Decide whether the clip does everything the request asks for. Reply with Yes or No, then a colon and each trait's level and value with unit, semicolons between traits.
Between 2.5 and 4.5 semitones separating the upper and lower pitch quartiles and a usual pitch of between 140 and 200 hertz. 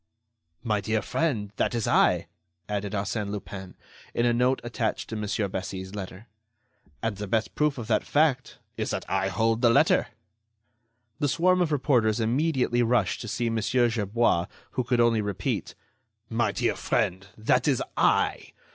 No: average, 3.2 semitones; low, 115 Hz